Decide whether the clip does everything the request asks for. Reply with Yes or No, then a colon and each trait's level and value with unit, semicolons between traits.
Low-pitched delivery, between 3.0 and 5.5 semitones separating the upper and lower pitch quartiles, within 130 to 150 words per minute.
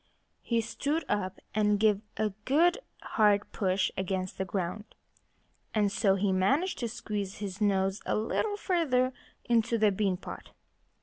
No: high, 210 Hz; average, 3.5 semitones; average, 145 wpm